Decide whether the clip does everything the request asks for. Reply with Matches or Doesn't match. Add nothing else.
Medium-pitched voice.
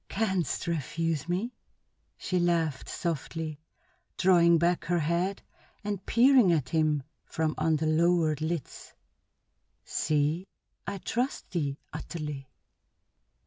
Matches